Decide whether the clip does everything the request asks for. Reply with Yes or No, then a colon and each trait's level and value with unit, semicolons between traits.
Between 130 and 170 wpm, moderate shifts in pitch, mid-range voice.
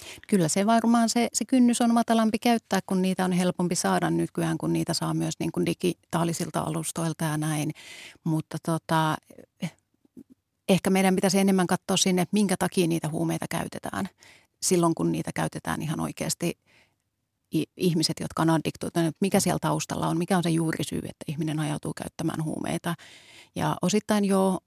Yes: fast, 155 wpm; average, 3.1 semitones; medium, 175 Hz